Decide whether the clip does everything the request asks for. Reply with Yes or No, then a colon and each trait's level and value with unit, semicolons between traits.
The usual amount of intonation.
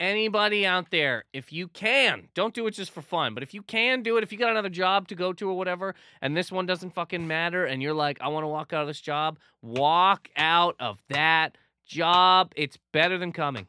Yes: average, 4.0 semitones